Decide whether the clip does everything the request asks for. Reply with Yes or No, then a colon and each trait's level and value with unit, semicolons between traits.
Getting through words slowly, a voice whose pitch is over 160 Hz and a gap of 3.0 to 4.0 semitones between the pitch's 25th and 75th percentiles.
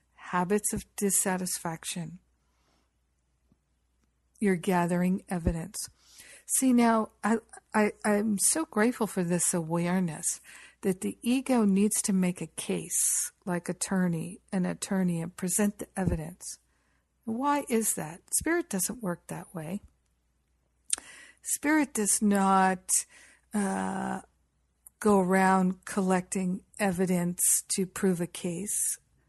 Yes: slow, 105 wpm; medium, 185 Hz; average, 3.5 semitones